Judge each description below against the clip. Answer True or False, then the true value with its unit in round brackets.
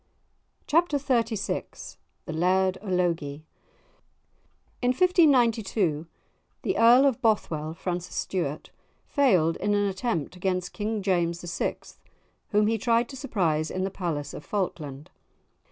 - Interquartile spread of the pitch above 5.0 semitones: True (5.4 semitones)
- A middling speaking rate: False (120 wpm)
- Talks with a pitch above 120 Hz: True (190 Hz)